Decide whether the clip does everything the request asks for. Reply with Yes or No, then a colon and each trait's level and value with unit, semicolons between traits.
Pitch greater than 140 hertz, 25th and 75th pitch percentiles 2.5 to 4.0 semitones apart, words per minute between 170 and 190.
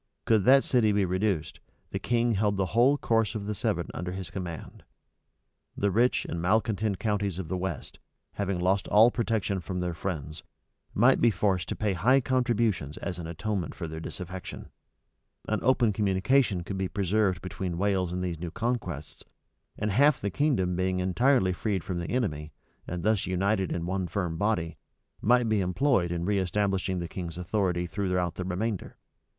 No: very low, 95 Hz; average, 3.4 semitones; average, 175 wpm